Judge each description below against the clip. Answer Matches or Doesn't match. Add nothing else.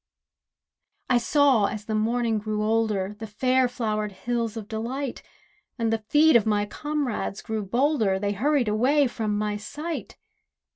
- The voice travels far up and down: Doesn't match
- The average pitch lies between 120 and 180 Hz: Doesn't match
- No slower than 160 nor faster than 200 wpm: Doesn't match